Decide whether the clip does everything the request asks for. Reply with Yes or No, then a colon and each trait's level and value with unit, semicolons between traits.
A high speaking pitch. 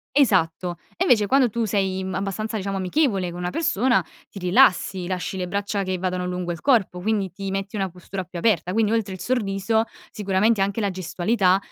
Yes: high, 195 Hz